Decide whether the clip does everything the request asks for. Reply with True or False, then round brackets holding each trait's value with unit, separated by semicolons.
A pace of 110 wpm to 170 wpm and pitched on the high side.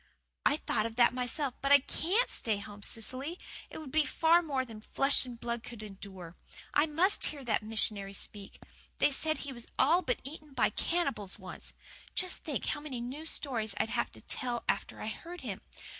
False (190 wpm; 255 Hz)